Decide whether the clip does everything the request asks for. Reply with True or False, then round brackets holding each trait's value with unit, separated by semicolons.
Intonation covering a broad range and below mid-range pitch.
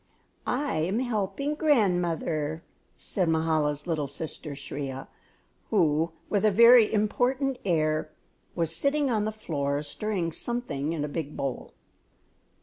False (6.4 semitones; 170 Hz)